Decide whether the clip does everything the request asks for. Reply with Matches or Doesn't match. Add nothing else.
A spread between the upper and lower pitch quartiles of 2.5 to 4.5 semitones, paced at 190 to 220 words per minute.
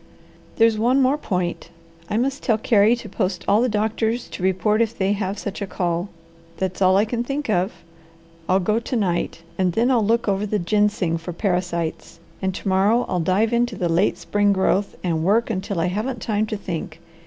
Matches